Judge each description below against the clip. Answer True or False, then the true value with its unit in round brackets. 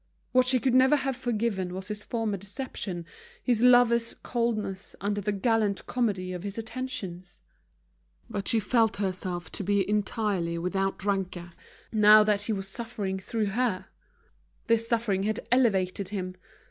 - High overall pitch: True (210 Hz)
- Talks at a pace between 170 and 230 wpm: False (145 wpm)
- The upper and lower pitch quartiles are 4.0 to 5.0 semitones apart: False (3.5 semitones)